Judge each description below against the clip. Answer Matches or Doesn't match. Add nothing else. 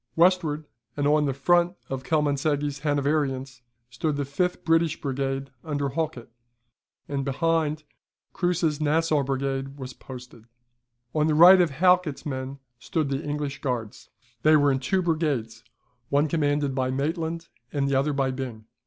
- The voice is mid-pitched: Matches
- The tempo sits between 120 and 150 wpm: Matches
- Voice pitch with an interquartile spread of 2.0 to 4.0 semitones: Matches